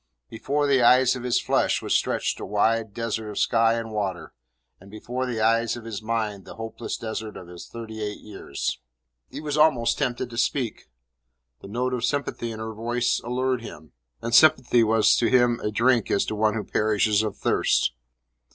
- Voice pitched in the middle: No, low, 115 Hz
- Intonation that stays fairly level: Yes, narrow, 2.3 semitones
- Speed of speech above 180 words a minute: Yes, average, 190 wpm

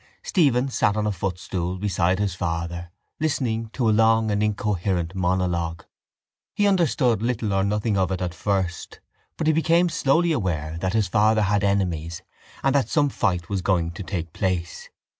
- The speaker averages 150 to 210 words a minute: Yes, average, 170 wpm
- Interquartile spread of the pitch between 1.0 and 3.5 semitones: No, average, 4.2 semitones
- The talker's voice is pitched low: Yes, low, 100 Hz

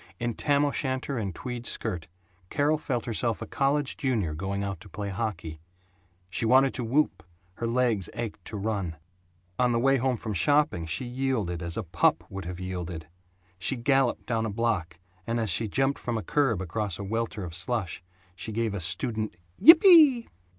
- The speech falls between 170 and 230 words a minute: Yes, average, 180 wpm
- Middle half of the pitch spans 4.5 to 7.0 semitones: Yes, wide, 5.6 semitones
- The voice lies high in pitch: No, low, 115 Hz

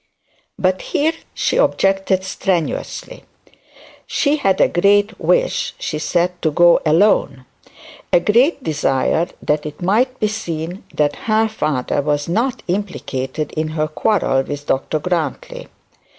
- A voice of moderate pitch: Yes, medium, 175 Hz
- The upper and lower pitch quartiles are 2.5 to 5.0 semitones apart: No, wide, 5.4 semitones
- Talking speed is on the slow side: Yes, slow, 130 wpm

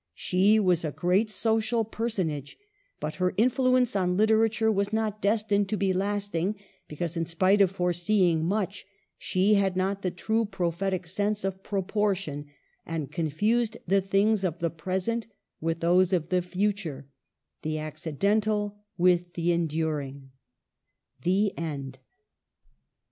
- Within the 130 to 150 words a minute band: Yes, average, 140 wpm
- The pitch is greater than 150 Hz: Yes, high, 190 Hz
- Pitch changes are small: No, average, 3.8 semitones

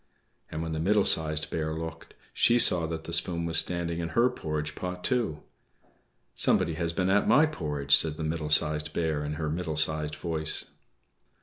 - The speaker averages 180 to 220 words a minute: Yes, average, 185 wpm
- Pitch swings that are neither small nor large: No, narrow, 2.1 semitones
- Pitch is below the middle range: Yes, very low, 80 Hz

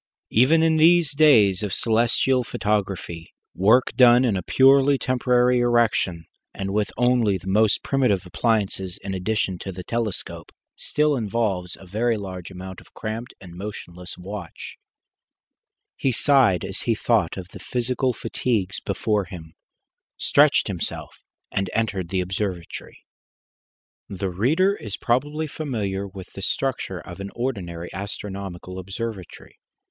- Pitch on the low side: Yes, low, 105 Hz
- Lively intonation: No, average, 4.7 semitones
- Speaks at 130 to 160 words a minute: Yes, slow, 135 wpm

